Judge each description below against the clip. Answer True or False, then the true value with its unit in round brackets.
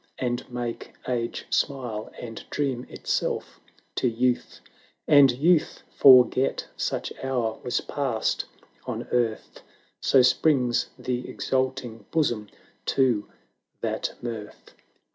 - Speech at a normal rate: False (105 wpm)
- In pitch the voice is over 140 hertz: False (125 Hz)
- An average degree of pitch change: False (2.2 semitones)